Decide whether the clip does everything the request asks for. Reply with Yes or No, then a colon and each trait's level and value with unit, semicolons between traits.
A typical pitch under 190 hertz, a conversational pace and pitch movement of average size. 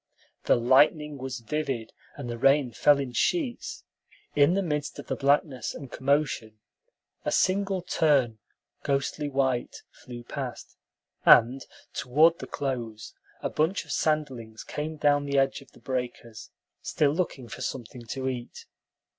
Yes: low, 135 Hz; average, 145 wpm; average, 3.5 semitones